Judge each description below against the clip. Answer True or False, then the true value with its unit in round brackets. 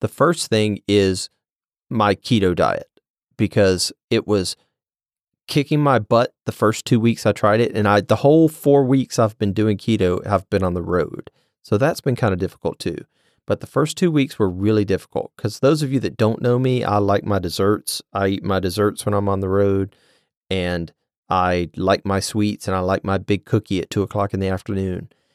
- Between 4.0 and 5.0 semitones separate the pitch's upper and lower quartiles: False (3.3 semitones)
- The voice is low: True (105 Hz)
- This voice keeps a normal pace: False (210 wpm)